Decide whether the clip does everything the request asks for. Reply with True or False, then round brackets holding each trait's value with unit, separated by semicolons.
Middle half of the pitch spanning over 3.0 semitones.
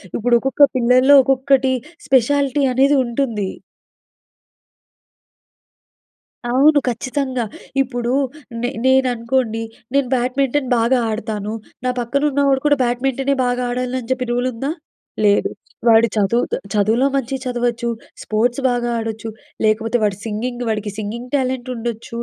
False (2.5 semitones)